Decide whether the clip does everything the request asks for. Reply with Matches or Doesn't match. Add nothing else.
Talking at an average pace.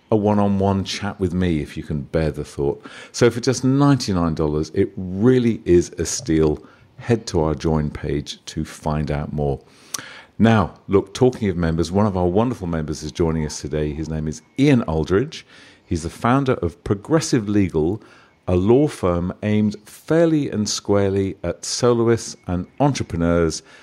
Matches